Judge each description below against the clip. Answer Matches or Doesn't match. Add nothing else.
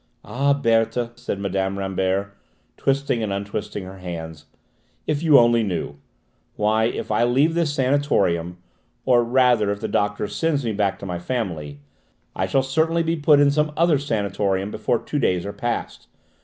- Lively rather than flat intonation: Matches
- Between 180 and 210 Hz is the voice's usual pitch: Doesn't match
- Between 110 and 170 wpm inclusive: Matches